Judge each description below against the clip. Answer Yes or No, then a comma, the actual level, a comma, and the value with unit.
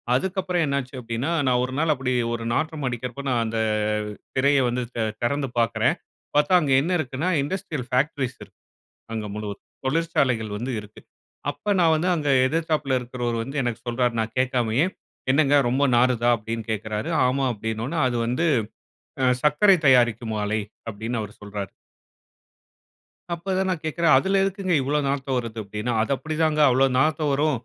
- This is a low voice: Yes, low, 130 Hz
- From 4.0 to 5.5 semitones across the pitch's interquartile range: Yes, average, 4.8 semitones